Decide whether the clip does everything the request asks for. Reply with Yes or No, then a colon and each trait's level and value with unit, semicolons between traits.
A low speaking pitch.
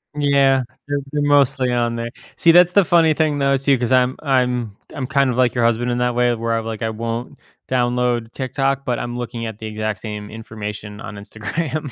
Yes: low, 125 Hz